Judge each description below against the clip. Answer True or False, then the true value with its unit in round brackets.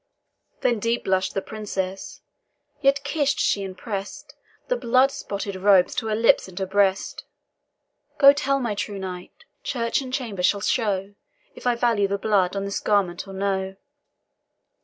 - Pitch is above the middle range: True (205 Hz)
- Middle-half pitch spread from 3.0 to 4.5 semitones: True (3.7 semitones)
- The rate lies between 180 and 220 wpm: False (160 wpm)